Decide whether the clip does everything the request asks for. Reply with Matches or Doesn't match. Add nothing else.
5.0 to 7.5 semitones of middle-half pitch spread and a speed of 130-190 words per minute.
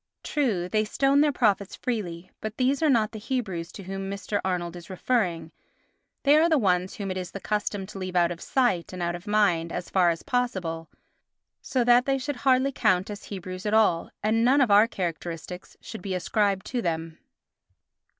Doesn't match